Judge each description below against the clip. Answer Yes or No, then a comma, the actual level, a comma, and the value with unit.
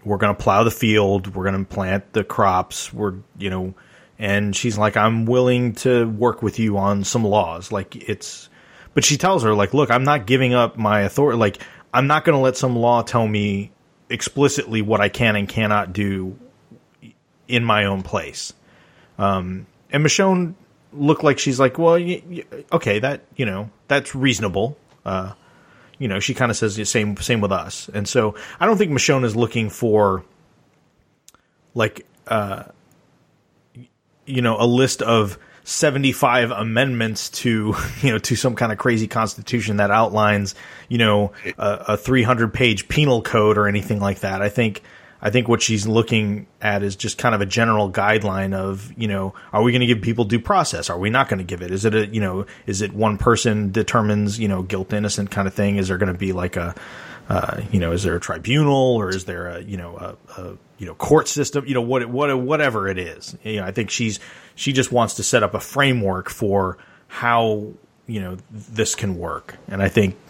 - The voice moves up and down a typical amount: Yes, average, 3.6 semitones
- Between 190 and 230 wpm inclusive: Yes, fast, 205 wpm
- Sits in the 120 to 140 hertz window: No, low, 110 Hz